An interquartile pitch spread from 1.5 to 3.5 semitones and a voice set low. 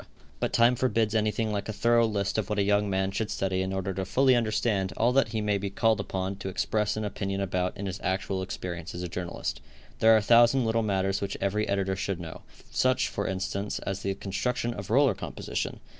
Yes: average, 2.7 semitones; low, 100 Hz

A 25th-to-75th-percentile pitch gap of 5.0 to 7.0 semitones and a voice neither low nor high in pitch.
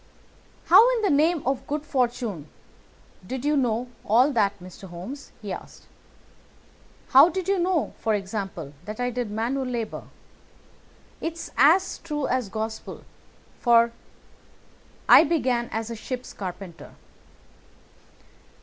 No: wide, 5.5 semitones; high, 245 Hz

